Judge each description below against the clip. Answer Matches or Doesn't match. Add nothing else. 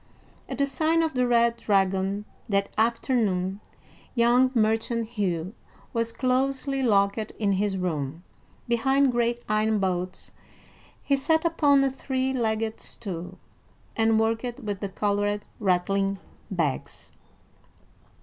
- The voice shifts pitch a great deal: Doesn't match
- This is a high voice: Matches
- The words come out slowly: Matches